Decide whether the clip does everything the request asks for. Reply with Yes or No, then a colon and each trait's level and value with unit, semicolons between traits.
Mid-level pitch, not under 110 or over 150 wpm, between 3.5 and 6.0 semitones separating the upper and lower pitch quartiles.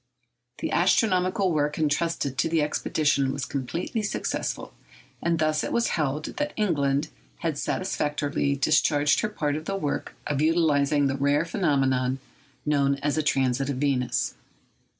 No: medium, 150 Hz; average, 145 wpm; average, 2.9 semitones